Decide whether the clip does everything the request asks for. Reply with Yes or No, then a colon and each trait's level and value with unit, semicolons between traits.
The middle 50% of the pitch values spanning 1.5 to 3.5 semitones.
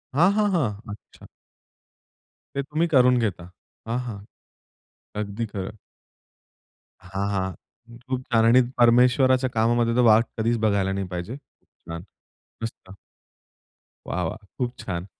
No: average, 4.2 semitones